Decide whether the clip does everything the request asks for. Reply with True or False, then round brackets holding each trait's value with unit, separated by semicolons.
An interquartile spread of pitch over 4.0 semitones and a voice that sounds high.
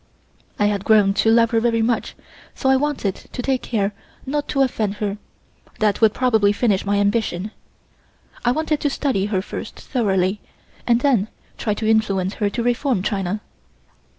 False (3.4 semitones; 220 Hz)